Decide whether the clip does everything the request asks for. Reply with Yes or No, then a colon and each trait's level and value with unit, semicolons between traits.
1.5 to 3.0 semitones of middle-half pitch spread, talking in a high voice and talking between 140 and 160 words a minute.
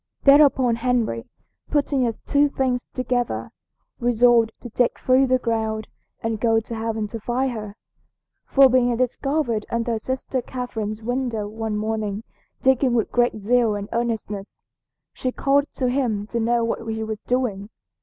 Yes: narrow, 2.5 semitones; high, 235 Hz; average, 150 wpm